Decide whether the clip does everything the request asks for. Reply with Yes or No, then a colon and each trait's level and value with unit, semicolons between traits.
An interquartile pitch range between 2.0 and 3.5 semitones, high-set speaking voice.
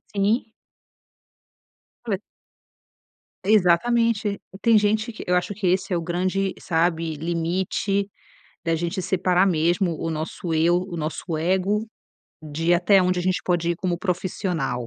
No: average, 2.8 semitones; medium, 180 Hz